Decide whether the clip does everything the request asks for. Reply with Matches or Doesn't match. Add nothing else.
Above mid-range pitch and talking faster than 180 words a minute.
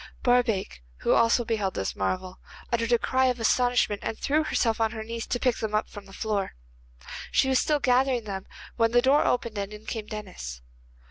Matches